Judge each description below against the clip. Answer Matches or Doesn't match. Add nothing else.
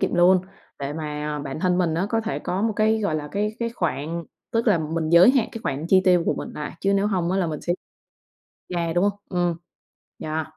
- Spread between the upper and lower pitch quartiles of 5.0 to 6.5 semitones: Doesn't match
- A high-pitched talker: Doesn't match